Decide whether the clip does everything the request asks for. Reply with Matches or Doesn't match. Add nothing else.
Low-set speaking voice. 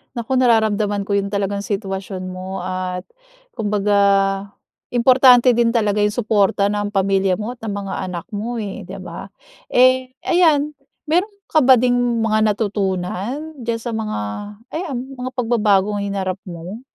Doesn't match